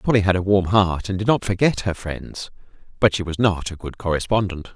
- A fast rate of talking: Yes, fast, 225 wpm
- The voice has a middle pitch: No, very low, 95 Hz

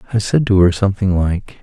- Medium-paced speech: No, fast, 220 wpm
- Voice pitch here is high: No, low, 100 Hz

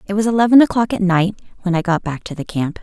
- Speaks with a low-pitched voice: No, high, 195 Hz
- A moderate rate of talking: No, fast, 275 wpm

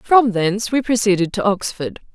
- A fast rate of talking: No, average, 170 wpm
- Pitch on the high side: Yes, high, 215 Hz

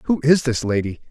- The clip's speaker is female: No, male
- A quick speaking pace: Yes, fast, 215 wpm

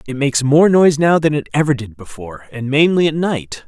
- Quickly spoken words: Yes, fast, 210 wpm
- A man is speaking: Yes, male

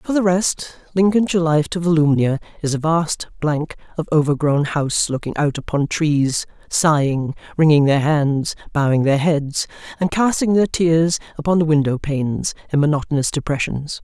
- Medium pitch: Yes, medium, 155 Hz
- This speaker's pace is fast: No, average, 155 wpm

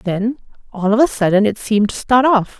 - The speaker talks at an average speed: No, fast, 230 wpm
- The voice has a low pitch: No, high, 220 Hz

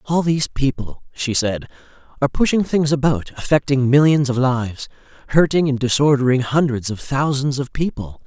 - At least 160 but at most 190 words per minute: No, average, 150 wpm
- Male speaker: Yes, male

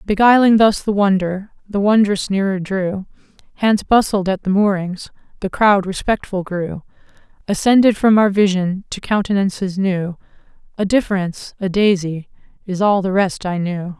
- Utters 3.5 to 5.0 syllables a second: Yes, 4.7 syllables/s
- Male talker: No, female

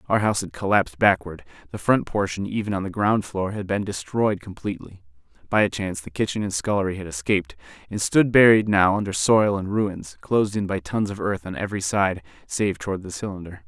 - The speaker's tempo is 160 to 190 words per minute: No, fast, 205 wpm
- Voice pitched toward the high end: No, very low, 95 Hz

